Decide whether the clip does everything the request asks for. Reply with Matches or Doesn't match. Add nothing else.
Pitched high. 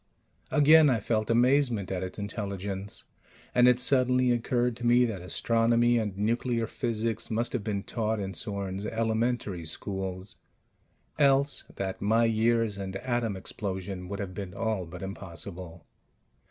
Doesn't match